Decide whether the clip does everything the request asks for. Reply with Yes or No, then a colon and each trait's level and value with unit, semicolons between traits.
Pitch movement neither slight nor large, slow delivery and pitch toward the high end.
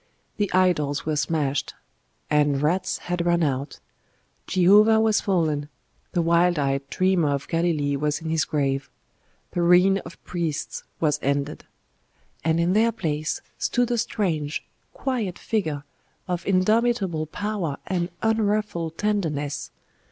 No: average, 4.6 semitones; slow, 130 wpm; medium, 170 Hz